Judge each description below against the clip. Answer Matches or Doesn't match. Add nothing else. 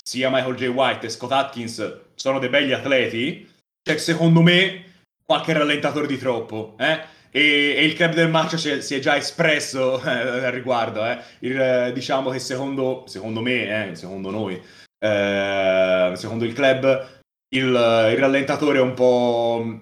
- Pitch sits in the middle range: Doesn't match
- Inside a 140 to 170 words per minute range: Matches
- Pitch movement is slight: Doesn't match